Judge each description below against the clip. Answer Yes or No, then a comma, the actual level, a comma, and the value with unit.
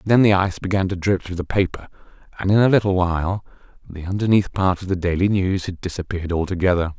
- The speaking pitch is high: No, very low, 95 Hz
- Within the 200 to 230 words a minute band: Yes, fast, 205 wpm